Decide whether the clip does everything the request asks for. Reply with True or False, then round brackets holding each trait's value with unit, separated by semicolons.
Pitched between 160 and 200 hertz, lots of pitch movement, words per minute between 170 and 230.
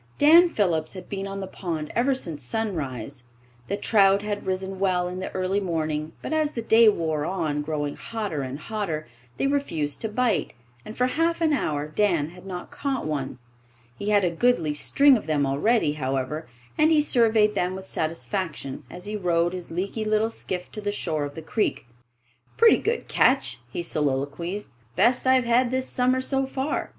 True (190 Hz; 6.8 semitones; 185 wpm)